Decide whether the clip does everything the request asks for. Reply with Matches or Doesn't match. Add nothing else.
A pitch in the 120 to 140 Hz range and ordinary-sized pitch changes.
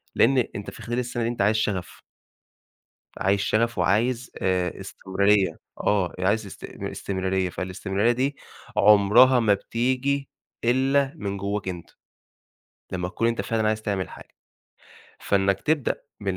Doesn't match